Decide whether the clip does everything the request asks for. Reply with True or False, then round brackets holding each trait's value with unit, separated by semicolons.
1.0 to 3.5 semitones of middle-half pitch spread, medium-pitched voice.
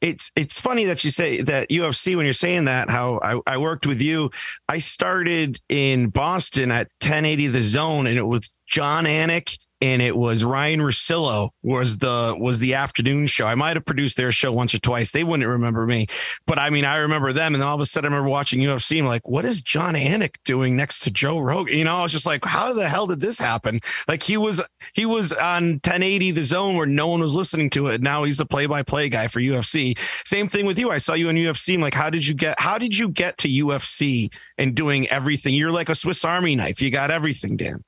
False (4.1 semitones; 145 Hz)